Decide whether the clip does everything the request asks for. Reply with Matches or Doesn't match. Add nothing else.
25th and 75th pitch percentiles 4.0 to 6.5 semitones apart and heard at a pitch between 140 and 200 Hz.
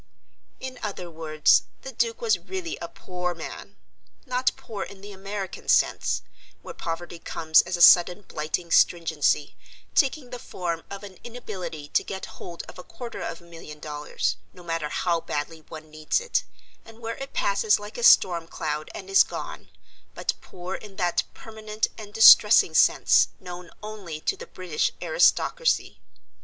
Matches